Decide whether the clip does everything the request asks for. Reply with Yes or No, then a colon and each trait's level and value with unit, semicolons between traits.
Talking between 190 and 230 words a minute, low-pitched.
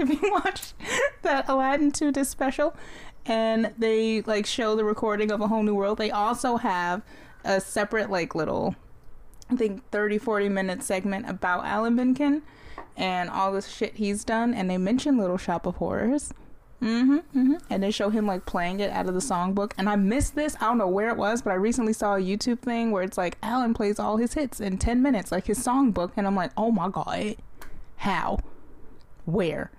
No: average, 200 wpm; high, 215 Hz